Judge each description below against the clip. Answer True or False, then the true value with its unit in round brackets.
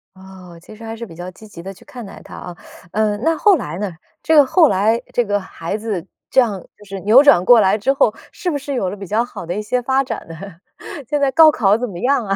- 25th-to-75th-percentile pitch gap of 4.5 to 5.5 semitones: True (5.2 semitones)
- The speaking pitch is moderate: False (215 Hz)